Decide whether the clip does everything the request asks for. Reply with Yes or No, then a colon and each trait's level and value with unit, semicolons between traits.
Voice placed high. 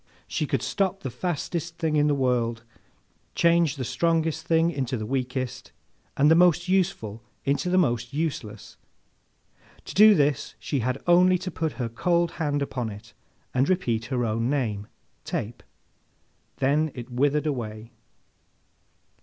No: medium, 140 Hz